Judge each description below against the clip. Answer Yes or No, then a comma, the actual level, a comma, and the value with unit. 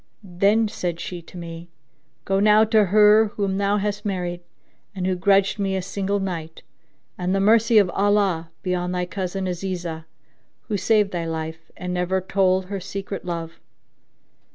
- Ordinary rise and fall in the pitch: No, narrow, 2.3 semitones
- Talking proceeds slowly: No, average, 165 wpm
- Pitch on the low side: No, high, 190 Hz